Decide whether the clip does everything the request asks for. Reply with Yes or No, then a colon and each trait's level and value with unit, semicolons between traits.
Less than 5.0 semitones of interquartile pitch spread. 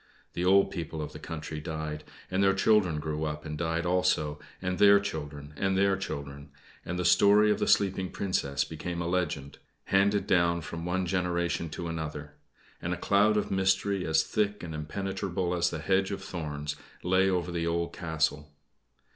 Yes: average, 3.7 semitones